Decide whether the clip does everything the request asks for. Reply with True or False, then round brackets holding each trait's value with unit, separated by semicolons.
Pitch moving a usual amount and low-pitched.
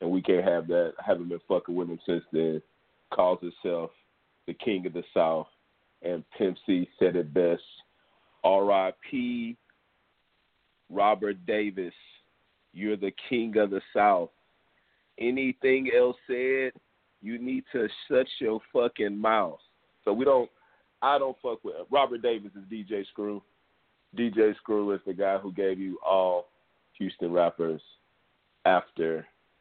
False (6.3 semitones; 100 Hz)